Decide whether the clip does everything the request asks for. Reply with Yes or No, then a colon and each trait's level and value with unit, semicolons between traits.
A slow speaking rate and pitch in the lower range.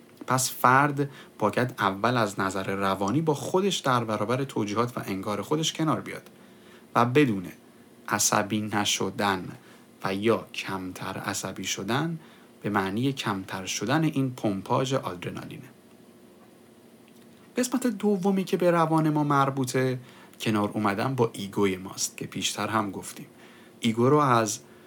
No: average, 125 wpm; low, 120 Hz